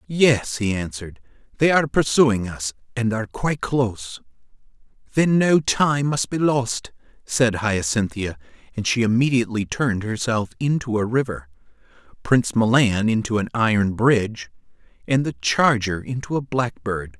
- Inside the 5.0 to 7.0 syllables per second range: No, 4.8 syllables/s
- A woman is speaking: No, male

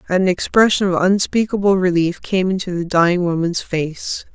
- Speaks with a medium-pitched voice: Yes, medium, 180 Hz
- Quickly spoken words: No, average, 150 wpm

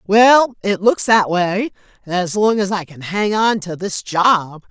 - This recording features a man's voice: No, female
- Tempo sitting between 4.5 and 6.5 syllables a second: No, 3.6 syllables/s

